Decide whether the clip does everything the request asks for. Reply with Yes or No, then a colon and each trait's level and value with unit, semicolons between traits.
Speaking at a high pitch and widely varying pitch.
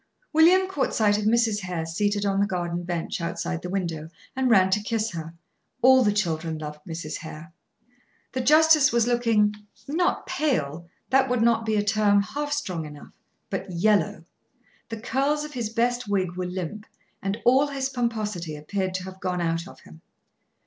Yes: high, 205 Hz; wide, 5.9 semitones